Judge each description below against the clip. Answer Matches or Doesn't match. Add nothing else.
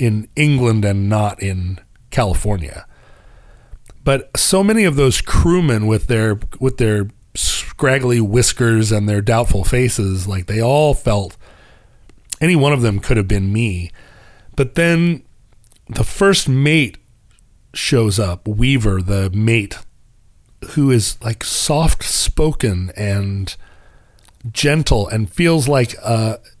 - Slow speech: Matches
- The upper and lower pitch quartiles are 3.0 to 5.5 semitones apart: Matches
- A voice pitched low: Matches